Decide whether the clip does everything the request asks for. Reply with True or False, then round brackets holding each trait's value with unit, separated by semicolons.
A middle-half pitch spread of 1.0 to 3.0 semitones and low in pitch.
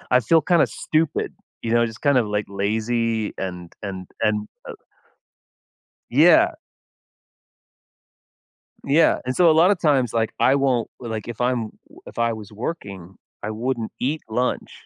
False (4.4 semitones; 120 Hz)